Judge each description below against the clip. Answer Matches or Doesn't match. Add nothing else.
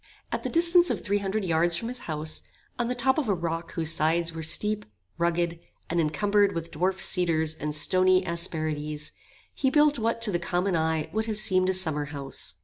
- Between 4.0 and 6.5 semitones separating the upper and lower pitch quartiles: Matches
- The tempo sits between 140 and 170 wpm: Doesn't match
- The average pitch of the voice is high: Doesn't match